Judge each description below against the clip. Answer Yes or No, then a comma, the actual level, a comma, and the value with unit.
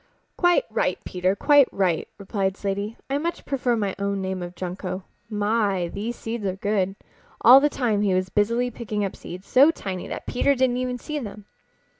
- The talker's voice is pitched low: No, high, 205 Hz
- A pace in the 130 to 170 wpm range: No, average, 185 wpm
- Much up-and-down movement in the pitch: No, average, 4.4 semitones